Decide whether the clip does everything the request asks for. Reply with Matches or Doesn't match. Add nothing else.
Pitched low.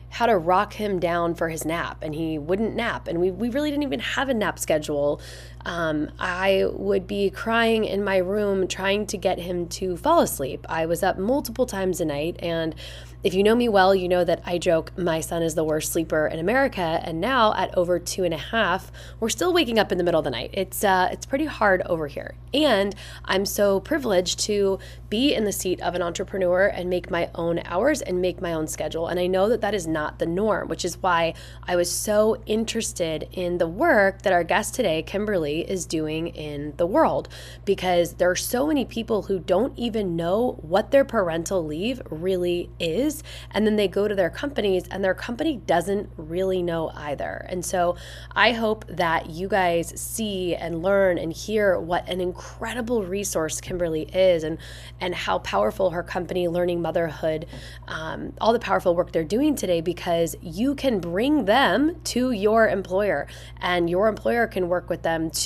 Doesn't match